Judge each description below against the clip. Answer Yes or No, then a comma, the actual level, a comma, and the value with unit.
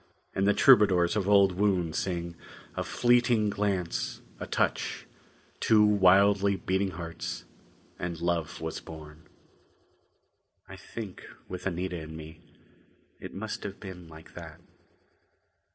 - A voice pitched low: Yes, very low, 95 Hz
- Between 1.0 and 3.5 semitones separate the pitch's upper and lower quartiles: Yes, average, 3.1 semitones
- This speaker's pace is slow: Yes, slow, 120 wpm